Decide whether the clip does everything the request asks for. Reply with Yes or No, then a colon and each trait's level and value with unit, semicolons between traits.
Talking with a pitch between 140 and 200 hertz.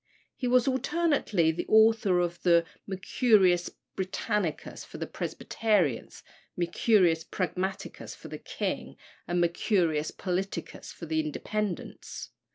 Yes: medium, 185 Hz